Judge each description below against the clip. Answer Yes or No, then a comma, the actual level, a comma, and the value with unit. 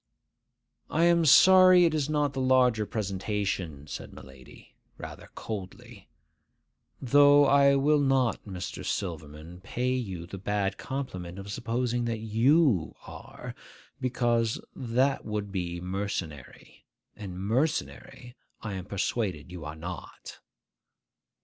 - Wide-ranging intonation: Yes, wide, 6.5 semitones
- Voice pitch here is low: Yes, low, 110 Hz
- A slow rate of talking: Yes, slow, 120 wpm